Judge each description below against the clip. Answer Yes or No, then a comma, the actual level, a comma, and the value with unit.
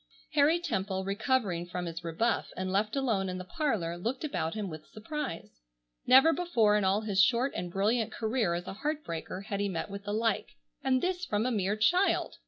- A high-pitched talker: Yes, high, 210 Hz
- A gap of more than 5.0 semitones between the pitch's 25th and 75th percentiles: Yes, wide, 5.6 semitones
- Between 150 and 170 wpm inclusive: No, average, 200 wpm